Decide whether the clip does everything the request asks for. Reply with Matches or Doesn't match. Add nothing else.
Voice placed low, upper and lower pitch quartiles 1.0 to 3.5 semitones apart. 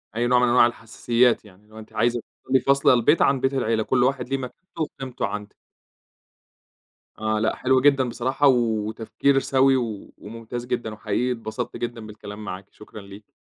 Matches